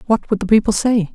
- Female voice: Yes, female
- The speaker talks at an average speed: No, fast, 260 wpm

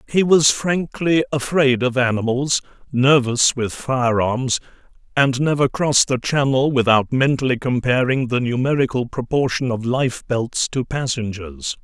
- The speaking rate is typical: No, slow, 120 wpm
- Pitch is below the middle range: Yes, low, 130 Hz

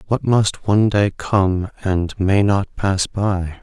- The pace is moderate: Yes, average, 165 wpm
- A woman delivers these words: No, male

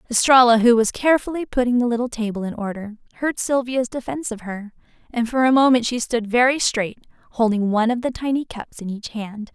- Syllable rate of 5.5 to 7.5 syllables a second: Yes, 5.9 syllables/s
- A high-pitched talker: Yes, high, 235 Hz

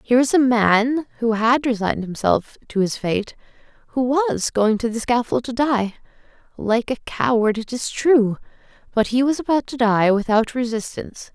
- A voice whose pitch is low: No, high, 235 Hz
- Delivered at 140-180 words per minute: Yes, average, 170 wpm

